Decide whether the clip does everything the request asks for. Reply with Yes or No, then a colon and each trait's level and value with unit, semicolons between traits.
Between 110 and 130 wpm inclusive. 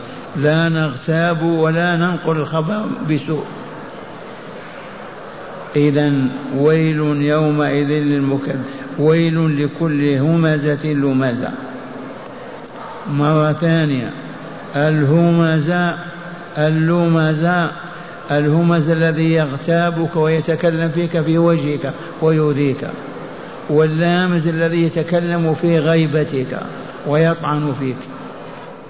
No: average, 70 wpm